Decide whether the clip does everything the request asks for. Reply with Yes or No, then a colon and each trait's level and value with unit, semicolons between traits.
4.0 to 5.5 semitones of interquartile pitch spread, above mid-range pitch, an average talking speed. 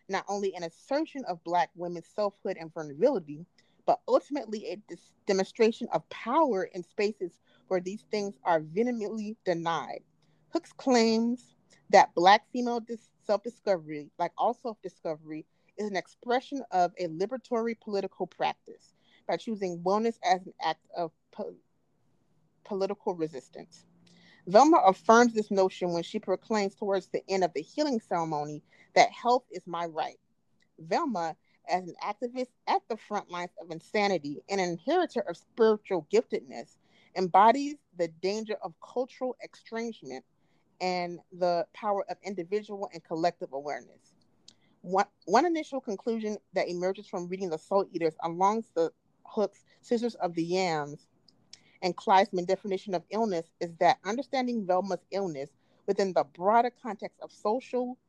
Yes: average, 4.6 semitones; high, 195 Hz; average, 145 wpm